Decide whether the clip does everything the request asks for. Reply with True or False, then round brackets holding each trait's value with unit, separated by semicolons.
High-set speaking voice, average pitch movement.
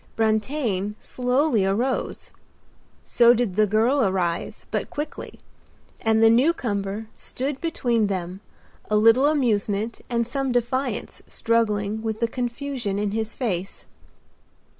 True (225 Hz; 3.4 semitones)